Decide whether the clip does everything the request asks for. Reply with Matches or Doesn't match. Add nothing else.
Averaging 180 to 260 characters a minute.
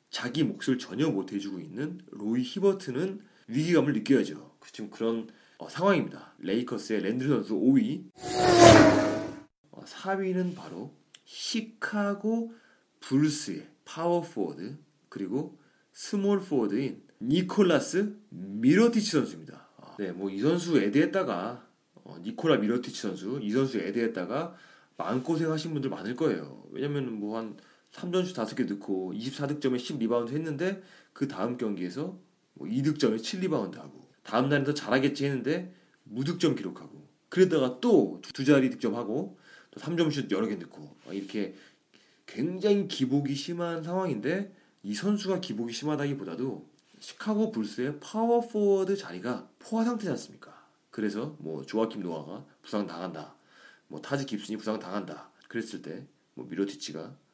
Doesn't match